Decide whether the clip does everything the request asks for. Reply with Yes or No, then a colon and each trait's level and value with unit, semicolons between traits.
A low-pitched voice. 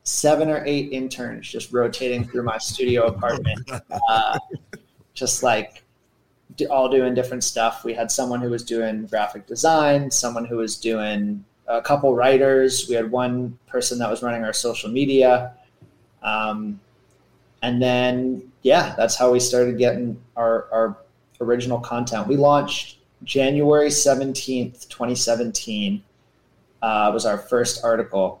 Yes: low, 125 Hz